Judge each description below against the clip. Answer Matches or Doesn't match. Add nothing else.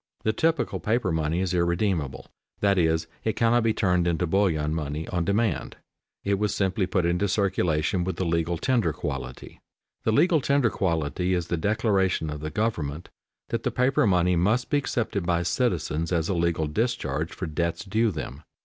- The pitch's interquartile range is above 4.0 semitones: Matches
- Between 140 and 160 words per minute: Doesn't match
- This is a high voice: Doesn't match